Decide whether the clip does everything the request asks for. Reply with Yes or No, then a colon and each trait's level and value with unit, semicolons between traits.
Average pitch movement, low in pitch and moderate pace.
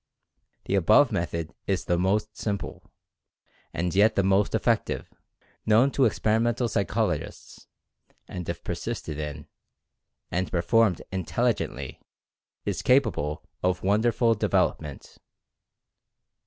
No: average, 4.5 semitones; low, 100 Hz; slow, 100 wpm